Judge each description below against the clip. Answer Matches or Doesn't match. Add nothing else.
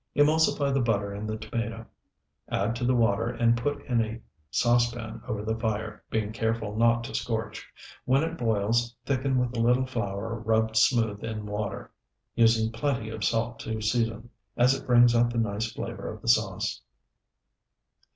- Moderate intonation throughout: Doesn't match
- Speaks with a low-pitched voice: Matches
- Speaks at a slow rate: Doesn't match